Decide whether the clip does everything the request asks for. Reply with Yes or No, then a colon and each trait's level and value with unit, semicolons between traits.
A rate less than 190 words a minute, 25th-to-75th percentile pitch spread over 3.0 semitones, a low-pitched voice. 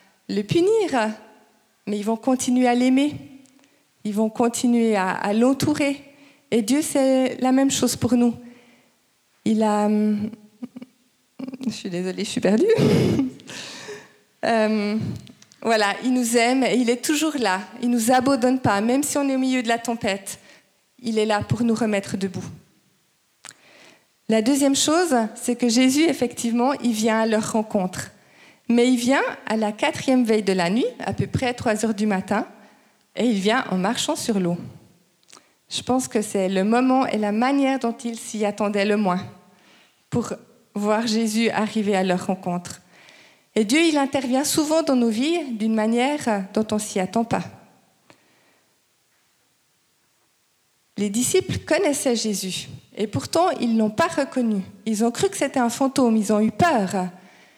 No: average, 160 wpm; average, 3.5 semitones; high, 235 Hz